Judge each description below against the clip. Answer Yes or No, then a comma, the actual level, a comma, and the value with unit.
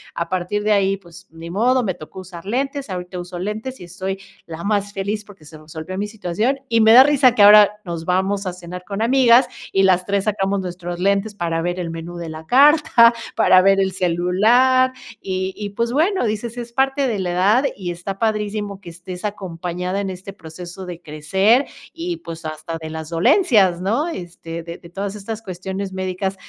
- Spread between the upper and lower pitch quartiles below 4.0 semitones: Yes, average, 3.6 semitones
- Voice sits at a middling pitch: No, high, 195 Hz